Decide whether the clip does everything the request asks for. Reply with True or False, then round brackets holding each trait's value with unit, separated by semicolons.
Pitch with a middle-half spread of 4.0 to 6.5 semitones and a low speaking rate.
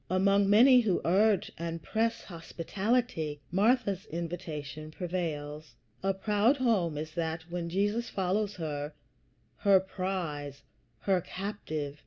True (4.4 semitones; 115 wpm)